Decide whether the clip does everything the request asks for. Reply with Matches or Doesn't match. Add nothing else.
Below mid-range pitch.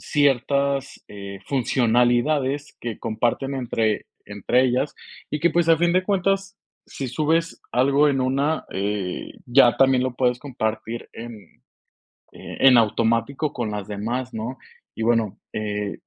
Matches